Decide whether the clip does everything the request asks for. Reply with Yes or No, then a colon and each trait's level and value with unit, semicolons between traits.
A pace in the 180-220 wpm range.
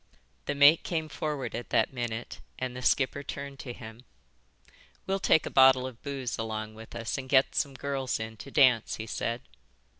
Yes: average, 185 wpm